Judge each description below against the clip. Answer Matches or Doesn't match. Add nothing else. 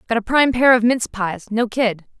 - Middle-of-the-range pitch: Doesn't match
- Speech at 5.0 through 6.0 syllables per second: Matches